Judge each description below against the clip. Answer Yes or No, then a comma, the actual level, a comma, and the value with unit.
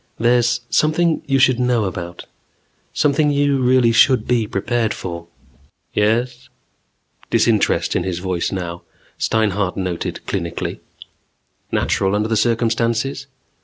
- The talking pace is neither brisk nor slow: No, slow, 115 wpm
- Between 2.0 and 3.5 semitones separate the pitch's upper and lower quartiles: No, average, 4.9 semitones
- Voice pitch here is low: Yes, low, 115 Hz